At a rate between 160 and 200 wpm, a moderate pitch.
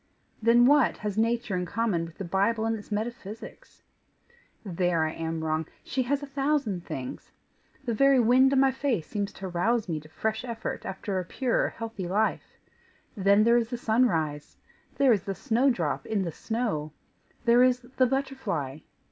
No: average, 175 wpm; high, 220 Hz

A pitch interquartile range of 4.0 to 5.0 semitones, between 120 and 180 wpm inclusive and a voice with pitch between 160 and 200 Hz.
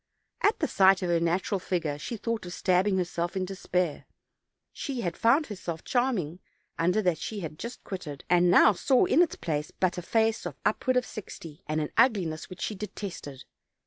No: average, 4.3 semitones; average, 195 wpm; medium, 185 Hz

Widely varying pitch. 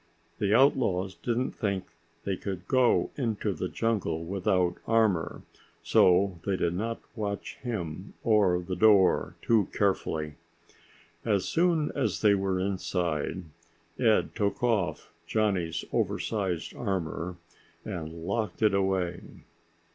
No: average, 3.6 semitones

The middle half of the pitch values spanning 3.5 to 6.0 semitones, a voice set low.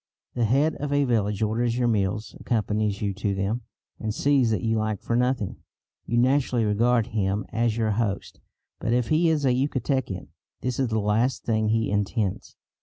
No: average, 3.0 semitones; low, 115 Hz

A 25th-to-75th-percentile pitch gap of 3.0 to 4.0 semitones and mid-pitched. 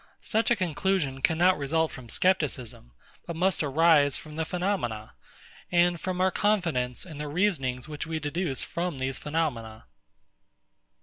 No: average, 5.0 semitones; medium, 160 Hz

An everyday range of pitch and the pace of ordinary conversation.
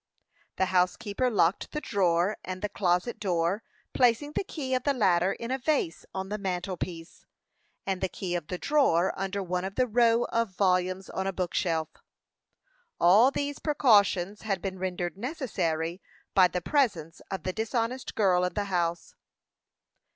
Yes: average, 4.4 semitones; average, 165 wpm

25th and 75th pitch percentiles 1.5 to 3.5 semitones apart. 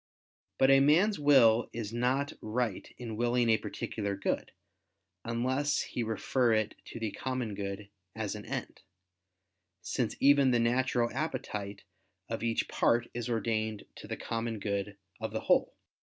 Yes: average, 2.9 semitones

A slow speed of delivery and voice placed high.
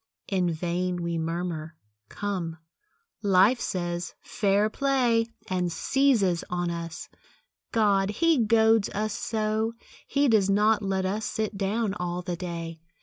Yes: slow, 130 wpm; high, 195 Hz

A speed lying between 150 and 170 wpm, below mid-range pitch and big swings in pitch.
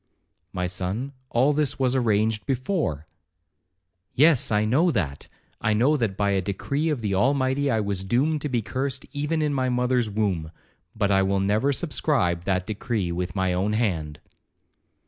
Yes: average, 165 wpm; low, 110 Hz; wide, 6.0 semitones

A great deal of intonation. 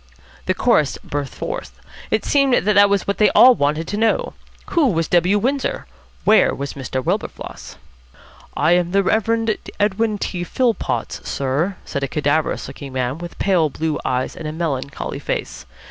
Yes: wide, 6.7 semitones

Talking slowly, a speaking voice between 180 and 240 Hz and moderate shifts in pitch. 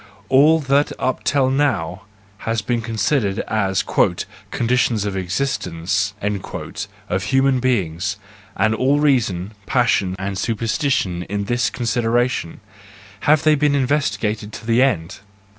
No: slow, 125 wpm; low, 110 Hz; average, 5.0 semitones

